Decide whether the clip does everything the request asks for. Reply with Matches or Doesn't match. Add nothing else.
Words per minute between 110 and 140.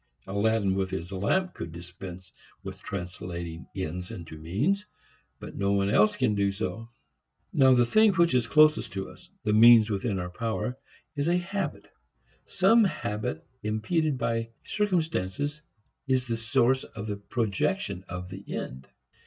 Doesn't match